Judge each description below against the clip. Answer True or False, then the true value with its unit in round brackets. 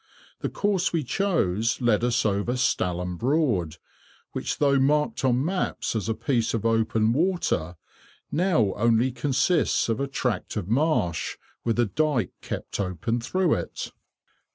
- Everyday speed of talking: True (145 wpm)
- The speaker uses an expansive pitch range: True (5.8 semitones)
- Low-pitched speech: True (120 Hz)